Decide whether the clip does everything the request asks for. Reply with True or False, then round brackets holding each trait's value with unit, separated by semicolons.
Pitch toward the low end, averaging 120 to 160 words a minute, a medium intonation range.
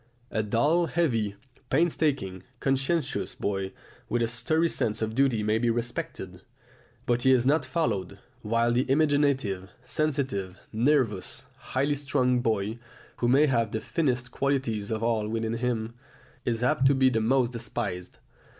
True (120 Hz; 145 wpm; 3.8 semitones)